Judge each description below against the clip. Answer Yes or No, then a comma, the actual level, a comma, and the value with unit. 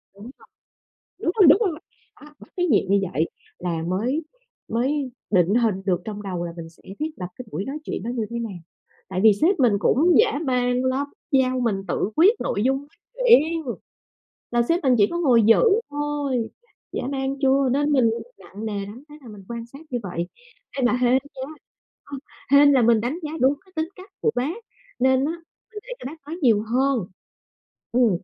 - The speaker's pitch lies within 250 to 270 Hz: Yes, very high, 255 Hz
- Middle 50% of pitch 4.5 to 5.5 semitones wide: Yes, average, 5.2 semitones